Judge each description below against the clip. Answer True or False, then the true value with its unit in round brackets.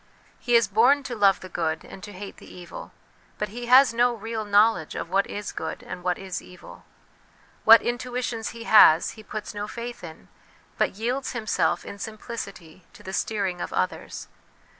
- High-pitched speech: True (210 Hz)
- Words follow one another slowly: False (185 wpm)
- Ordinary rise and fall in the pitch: True (3.9 semitones)